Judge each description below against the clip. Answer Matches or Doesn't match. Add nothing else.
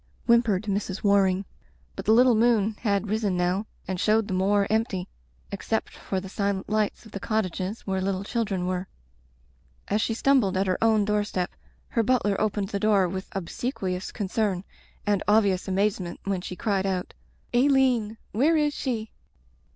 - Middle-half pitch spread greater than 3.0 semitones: Doesn't match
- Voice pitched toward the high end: Matches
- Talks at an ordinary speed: Matches